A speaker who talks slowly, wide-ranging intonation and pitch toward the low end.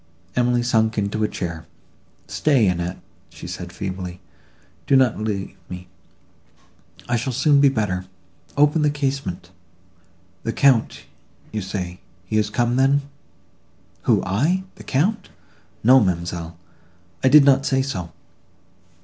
Yes: slow, 115 wpm; wide, 6.8 semitones; low, 110 Hz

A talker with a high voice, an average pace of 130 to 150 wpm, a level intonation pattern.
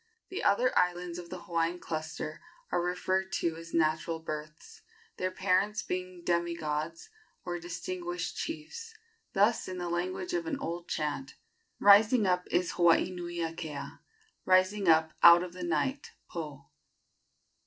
No: medium, 175 Hz; average, 145 wpm; narrow, 2.3 semitones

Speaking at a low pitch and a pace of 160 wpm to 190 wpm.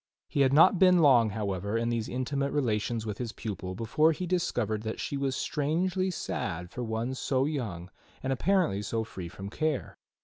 Yes: low, 125 Hz; average, 180 wpm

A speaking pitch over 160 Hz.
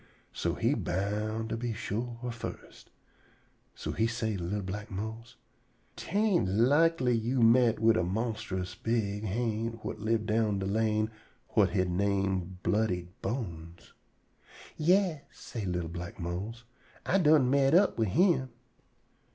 No: low, 110 Hz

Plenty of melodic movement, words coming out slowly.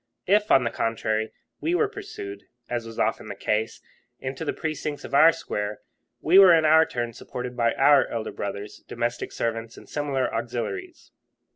No: wide, 5.8 semitones; average, 170 wpm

